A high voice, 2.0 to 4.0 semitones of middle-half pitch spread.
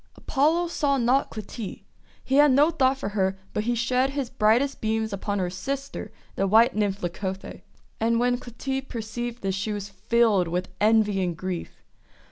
No: high, 225 Hz; average, 4.8 semitones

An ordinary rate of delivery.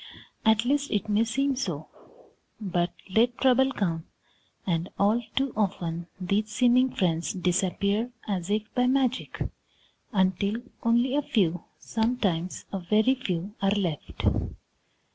No: slow, 125 wpm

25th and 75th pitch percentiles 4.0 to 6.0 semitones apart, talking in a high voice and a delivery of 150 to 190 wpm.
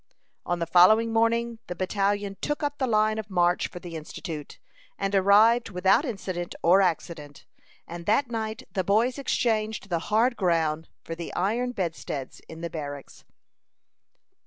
Yes: average, 4.7 semitones; high, 195 Hz; average, 155 wpm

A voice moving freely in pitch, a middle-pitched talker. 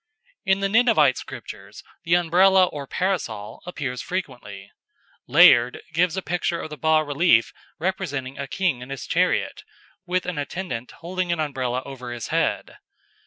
Yes: wide, 6.1 semitones; medium, 155 Hz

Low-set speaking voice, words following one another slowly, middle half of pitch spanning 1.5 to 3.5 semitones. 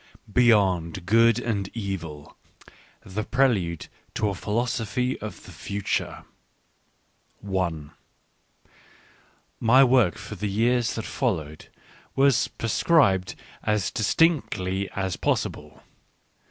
No: low, 105 Hz; slow, 100 wpm; average, 4.4 semitones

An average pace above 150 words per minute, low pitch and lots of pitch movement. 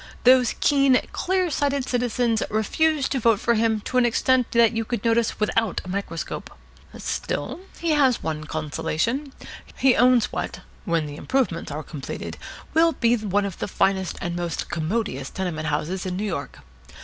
No: average, 160 wpm; high, 225 Hz; wide, 6.5 semitones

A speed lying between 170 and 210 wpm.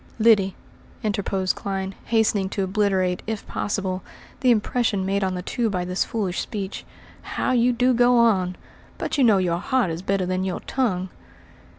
Yes: average, 175 wpm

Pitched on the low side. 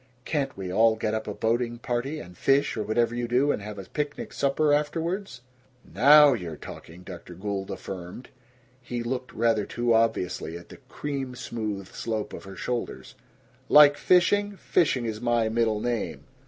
Yes: low, 120 Hz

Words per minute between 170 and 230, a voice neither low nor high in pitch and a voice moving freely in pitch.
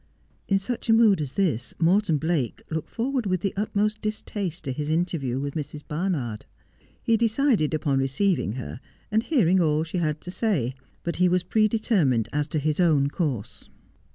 Yes: average, 180 wpm; medium, 170 Hz; wide, 6.0 semitones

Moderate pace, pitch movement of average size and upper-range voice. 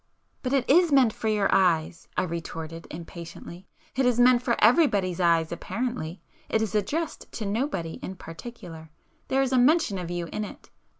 No: average, 160 wpm; wide, 6.7 semitones; high, 205 Hz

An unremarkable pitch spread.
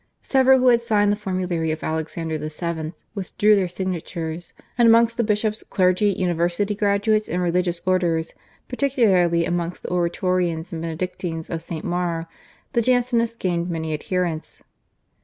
Yes: average, 3.8 semitones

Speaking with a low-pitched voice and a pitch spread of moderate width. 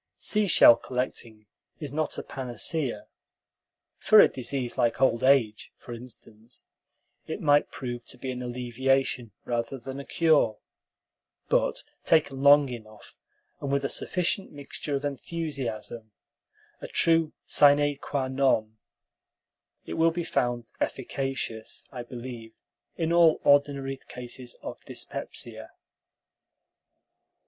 Yes: low, 130 Hz; average, 3.2 semitones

